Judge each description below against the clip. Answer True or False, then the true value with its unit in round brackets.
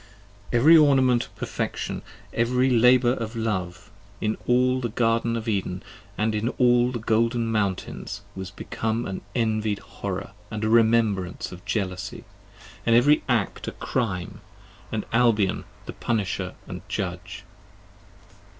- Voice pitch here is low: True (115 Hz)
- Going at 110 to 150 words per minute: True (135 wpm)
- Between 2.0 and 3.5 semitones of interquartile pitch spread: True (3.0 semitones)